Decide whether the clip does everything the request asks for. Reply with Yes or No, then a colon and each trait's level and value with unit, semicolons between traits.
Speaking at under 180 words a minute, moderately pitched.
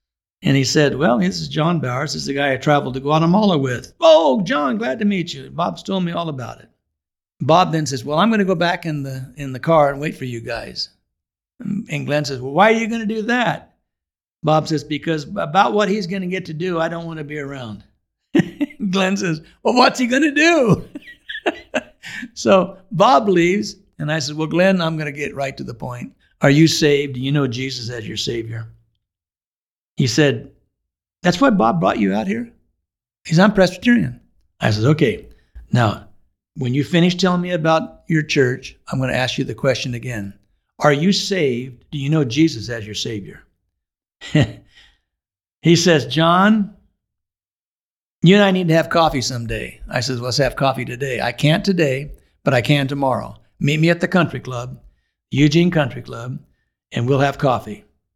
No: average, 195 wpm; medium, 150 Hz